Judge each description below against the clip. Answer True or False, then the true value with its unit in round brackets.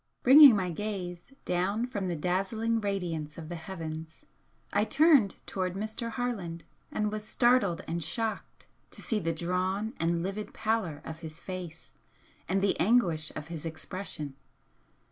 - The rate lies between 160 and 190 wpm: False (145 wpm)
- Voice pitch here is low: False (185 Hz)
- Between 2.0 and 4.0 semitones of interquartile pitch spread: False (4.5 semitones)